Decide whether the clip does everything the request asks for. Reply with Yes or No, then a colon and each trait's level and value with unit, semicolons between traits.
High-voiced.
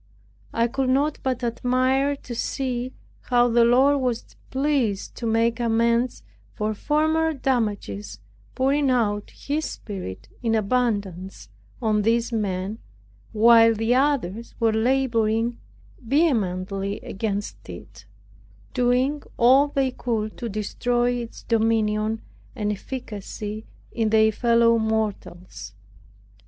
Yes: high, 230 Hz